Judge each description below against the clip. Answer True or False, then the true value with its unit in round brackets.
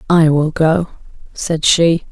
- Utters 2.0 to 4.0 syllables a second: True (3.4 syllables/s)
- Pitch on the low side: False (160 Hz)